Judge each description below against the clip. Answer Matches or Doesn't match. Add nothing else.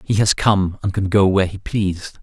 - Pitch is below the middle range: Matches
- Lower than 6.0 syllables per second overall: Matches